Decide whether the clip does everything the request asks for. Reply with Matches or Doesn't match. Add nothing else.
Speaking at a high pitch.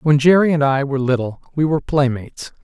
Doesn't match